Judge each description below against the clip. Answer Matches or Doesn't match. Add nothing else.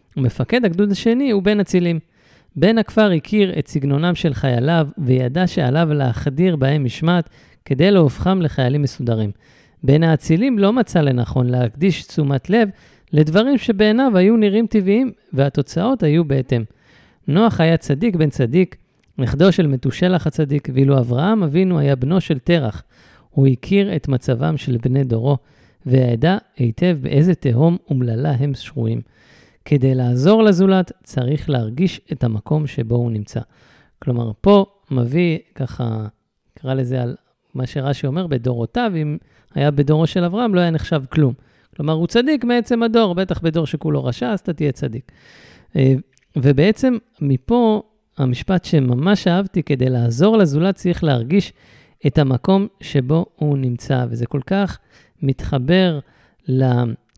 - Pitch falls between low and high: Matches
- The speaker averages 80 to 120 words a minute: Doesn't match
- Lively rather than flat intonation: Matches